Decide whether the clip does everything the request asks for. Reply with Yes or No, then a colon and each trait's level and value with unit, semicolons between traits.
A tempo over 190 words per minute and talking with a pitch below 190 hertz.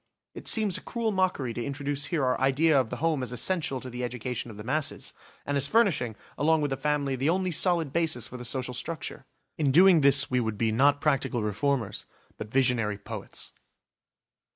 Yes: average, 200 wpm; low, 135 Hz